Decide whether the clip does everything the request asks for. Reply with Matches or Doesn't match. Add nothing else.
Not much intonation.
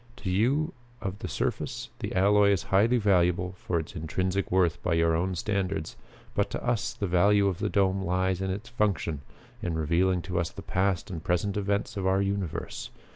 Matches